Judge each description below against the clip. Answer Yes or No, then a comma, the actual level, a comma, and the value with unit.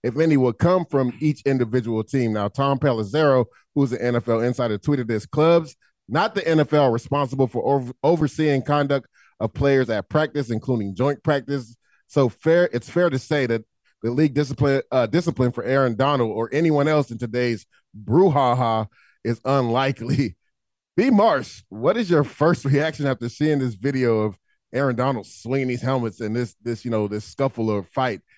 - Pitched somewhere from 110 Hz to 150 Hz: Yes, low, 135 Hz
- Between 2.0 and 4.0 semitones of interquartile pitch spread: Yes, average, 3.6 semitones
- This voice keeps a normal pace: Yes, average, 175 wpm